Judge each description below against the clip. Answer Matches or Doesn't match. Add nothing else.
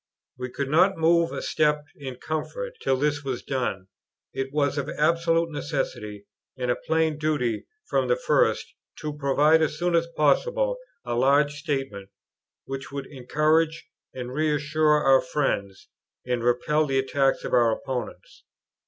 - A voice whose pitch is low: Doesn't match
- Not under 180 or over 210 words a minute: Doesn't match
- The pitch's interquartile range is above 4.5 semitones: Doesn't match